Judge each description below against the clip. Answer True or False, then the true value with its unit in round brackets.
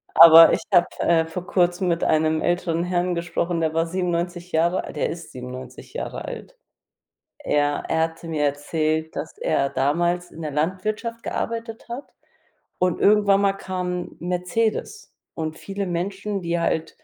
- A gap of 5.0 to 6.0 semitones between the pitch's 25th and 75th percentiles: False (2.6 semitones)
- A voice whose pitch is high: False (175 Hz)